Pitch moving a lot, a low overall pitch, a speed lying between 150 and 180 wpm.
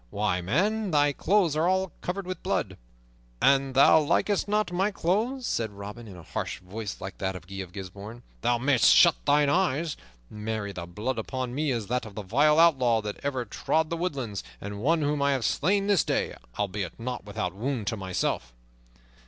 No: wide, 7.7 semitones; low, 130 Hz; average, 190 wpm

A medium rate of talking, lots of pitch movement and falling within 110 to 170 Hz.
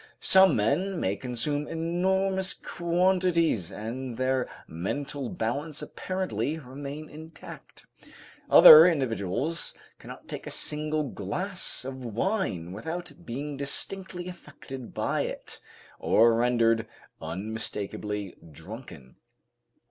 No: slow, 95 wpm; wide, 6.9 semitones; medium, 140 Hz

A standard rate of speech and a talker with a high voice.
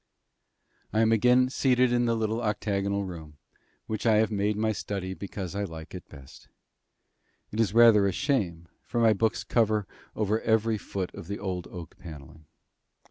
No: average, 170 wpm; low, 105 Hz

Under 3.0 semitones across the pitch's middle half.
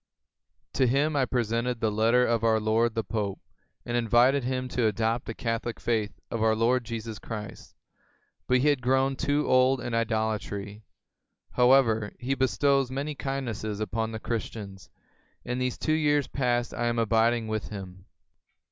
Yes: narrow, 2.6 semitones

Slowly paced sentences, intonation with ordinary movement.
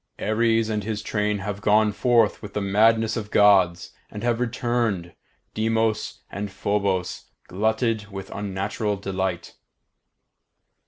No: slow, 120 wpm; narrow, 2.2 semitones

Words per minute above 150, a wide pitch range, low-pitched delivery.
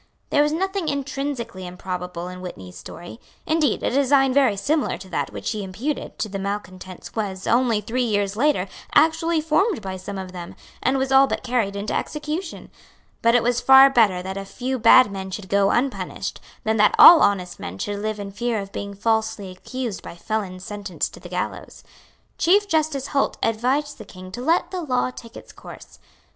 No: average, 190 wpm; wide, 5.9 semitones; high, 225 Hz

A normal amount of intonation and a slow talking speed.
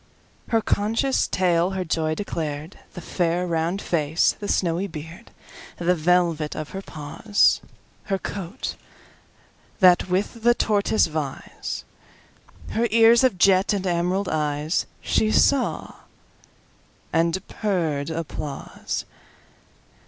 Yes: average, 3.9 semitones; slow, 95 wpm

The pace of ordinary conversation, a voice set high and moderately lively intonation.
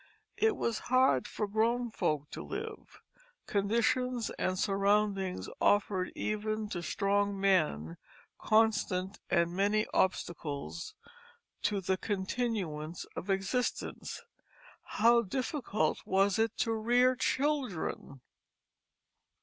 No: slow, 100 wpm; high, 205 Hz; average, 3.8 semitones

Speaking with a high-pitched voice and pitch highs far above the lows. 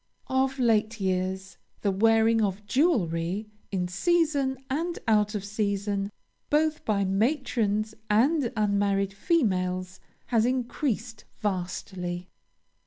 No: high, 210 Hz; average, 4.6 semitones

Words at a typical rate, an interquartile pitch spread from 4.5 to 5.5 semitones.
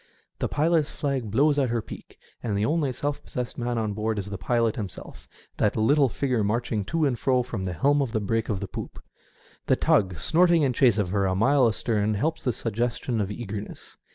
No: fast, 220 wpm; average, 4.8 semitones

